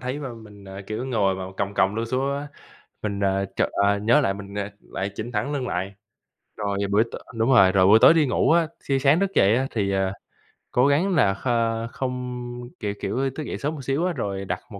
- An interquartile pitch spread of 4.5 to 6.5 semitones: Yes, average, 5.1 semitones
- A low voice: Yes, low, 115 Hz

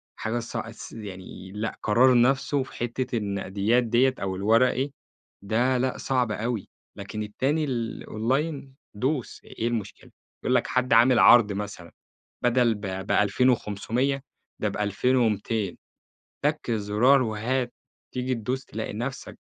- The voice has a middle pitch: No, low, 115 Hz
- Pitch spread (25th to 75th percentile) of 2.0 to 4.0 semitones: Yes, average, 3.5 semitones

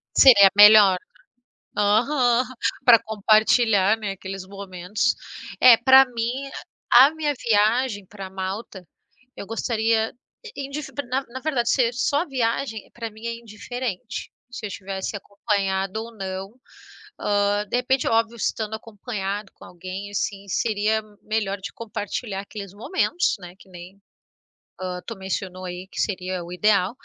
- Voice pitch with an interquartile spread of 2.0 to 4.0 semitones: Yes, average, 3.3 semitones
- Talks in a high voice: Yes, high, 210 Hz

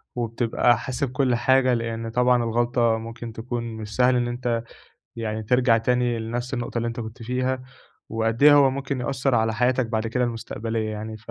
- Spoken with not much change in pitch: Yes, narrow, 1.8 semitones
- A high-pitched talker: No, low, 120 Hz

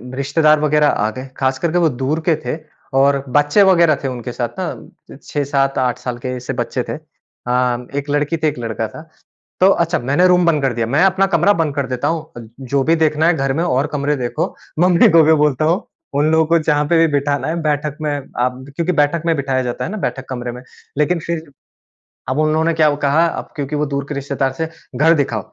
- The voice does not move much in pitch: No, average, 3.2 semitones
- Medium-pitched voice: Yes, medium, 145 Hz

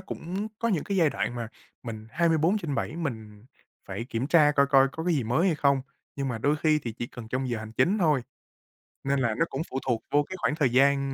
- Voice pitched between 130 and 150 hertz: Yes, medium, 140 Hz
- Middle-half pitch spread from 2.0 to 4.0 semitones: No, average, 5.1 semitones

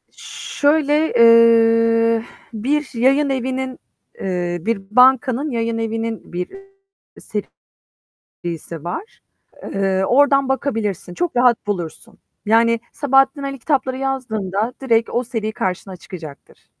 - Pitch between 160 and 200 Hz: No, high, 230 Hz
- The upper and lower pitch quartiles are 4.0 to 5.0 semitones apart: Yes, average, 4.3 semitones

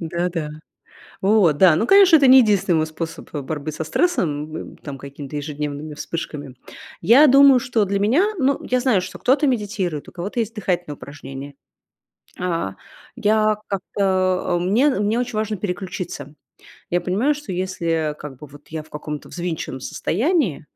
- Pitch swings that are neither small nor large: No, wide, 6.3 semitones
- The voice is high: No, medium, 180 Hz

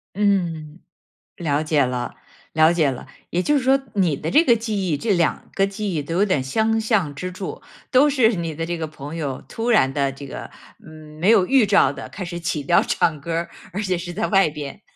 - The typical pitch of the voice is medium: Yes, medium, 175 Hz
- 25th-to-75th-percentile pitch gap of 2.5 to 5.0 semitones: No, wide, 5.4 semitones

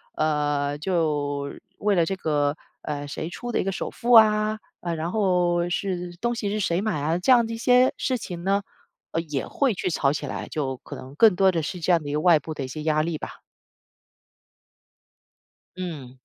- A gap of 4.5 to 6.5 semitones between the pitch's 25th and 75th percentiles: Yes, average, 5.0 semitones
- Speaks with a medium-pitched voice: Yes, medium, 170 Hz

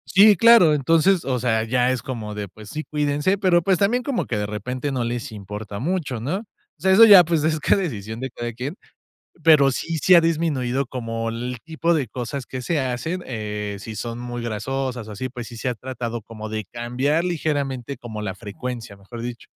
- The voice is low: Yes, low, 125 Hz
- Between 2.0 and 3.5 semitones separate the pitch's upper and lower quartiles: No, wide, 5.6 semitones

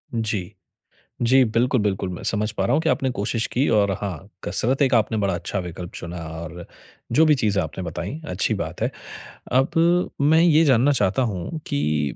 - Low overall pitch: Yes, low, 105 Hz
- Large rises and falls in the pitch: Yes, wide, 6.6 semitones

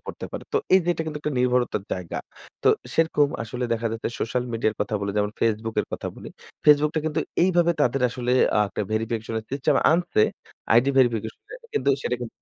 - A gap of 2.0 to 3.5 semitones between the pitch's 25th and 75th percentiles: No, average, 4.9 semitones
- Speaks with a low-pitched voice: Yes, low, 125 Hz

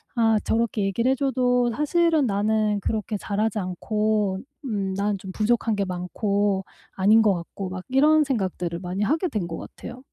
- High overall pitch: Yes, high, 210 Hz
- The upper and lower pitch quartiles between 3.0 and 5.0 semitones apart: Yes, average, 3.7 semitones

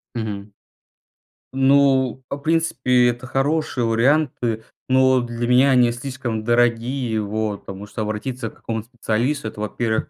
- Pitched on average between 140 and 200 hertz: No, low, 120 Hz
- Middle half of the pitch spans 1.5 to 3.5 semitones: Yes, average, 2.9 semitones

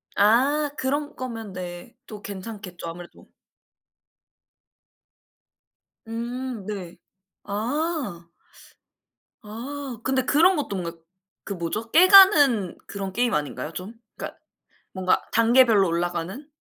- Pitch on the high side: Yes, high, 225 Hz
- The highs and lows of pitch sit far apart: Yes, wide, 6.1 semitones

